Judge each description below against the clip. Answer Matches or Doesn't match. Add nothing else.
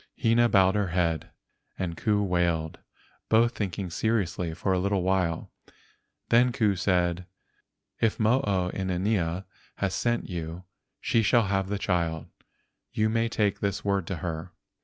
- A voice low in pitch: Matches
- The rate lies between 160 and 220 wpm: Doesn't match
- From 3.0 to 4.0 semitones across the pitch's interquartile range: Matches